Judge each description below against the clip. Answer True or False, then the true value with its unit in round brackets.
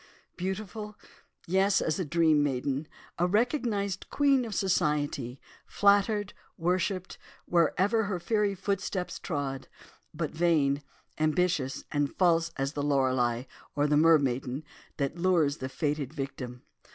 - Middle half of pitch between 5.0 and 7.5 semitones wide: True (5.4 semitones)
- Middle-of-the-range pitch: True (165 Hz)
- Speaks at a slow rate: True (120 wpm)